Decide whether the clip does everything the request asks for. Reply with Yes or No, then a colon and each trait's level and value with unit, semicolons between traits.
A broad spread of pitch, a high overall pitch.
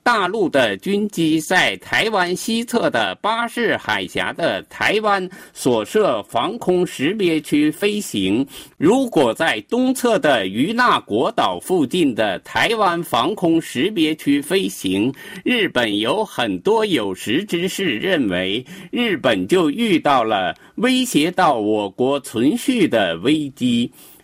Yes: wide, 6.5 semitones; high, 205 Hz